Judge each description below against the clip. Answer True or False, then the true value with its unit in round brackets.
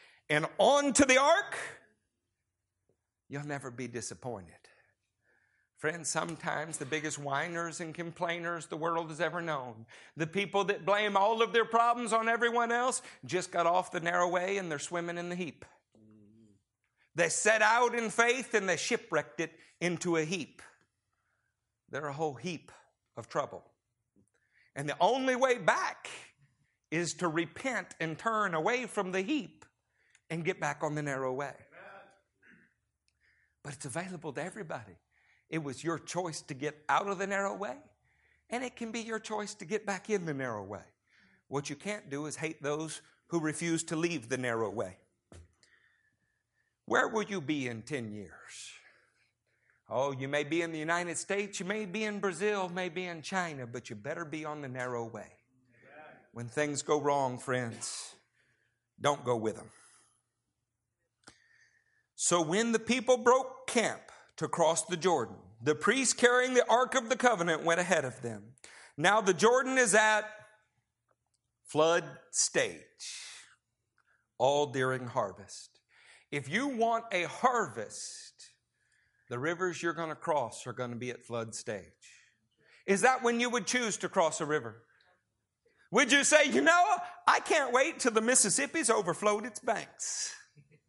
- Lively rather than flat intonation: True (7.1 semitones)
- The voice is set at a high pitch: False (170 Hz)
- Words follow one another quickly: False (160 wpm)